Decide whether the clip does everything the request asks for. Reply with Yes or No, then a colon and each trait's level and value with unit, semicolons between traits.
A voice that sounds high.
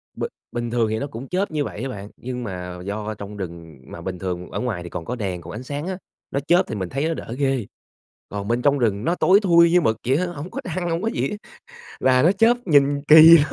No: low, 125 Hz